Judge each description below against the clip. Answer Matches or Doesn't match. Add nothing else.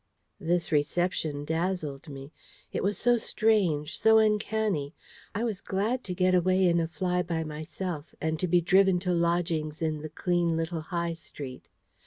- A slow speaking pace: Doesn't match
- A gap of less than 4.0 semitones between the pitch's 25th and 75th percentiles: Matches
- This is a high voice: Doesn't match